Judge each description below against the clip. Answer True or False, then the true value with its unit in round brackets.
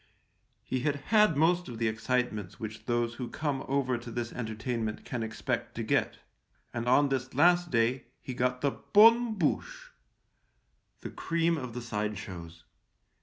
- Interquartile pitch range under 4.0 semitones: False (4.9 semitones)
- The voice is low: True (125 Hz)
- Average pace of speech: True (165 wpm)